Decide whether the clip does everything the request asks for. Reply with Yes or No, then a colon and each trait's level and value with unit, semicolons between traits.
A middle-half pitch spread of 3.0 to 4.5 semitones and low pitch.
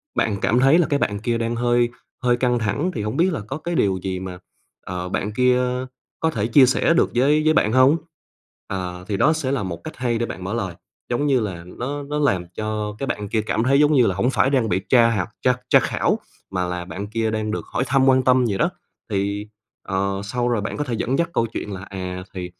No: average, 5.0 semitones; low, 115 Hz